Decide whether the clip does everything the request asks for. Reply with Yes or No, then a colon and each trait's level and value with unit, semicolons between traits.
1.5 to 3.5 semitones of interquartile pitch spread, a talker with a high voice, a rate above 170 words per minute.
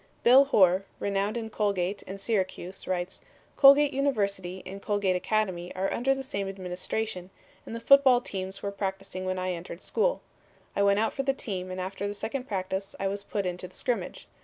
Yes: average, 3.1 semitones; high, 200 Hz; average, 185 wpm